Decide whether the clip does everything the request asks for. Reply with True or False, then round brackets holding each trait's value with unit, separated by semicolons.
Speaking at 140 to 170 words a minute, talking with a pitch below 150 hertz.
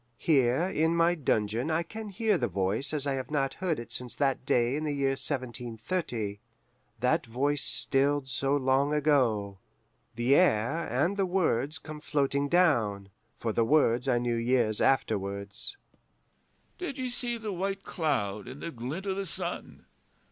True (160 wpm; 140 Hz)